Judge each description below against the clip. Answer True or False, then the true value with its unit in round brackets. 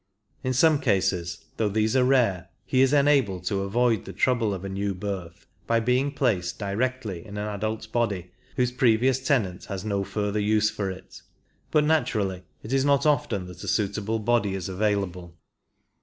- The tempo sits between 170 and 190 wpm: True (180 wpm)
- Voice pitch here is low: True (105 Hz)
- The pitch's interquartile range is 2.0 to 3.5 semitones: False (4.4 semitones)